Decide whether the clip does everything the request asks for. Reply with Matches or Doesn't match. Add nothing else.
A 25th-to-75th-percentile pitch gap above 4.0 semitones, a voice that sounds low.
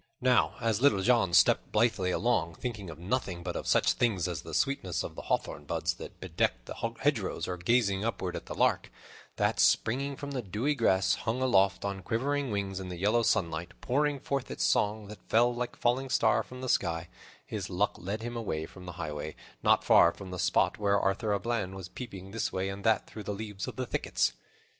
Matches